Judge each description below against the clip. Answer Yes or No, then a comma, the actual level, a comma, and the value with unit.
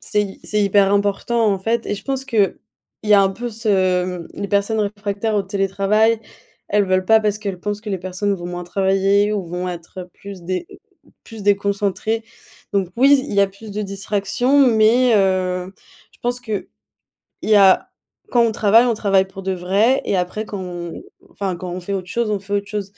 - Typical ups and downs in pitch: No, narrow, 2.2 semitones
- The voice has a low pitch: No, high, 200 Hz